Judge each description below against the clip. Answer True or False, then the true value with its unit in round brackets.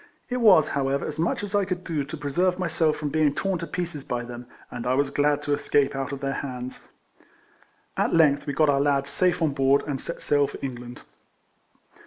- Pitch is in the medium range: True (145 Hz)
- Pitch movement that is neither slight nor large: True (3.3 semitones)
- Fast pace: True (215 wpm)